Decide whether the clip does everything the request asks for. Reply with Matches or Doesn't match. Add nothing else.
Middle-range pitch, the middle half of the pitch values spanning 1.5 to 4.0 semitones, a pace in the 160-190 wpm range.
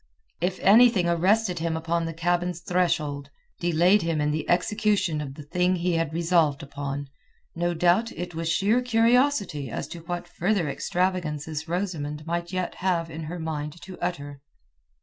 Matches